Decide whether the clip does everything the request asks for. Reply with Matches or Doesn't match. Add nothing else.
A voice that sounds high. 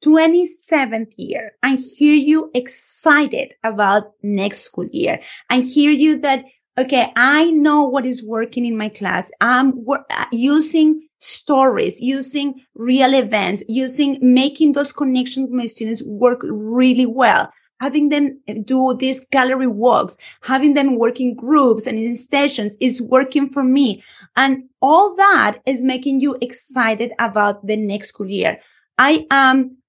Matches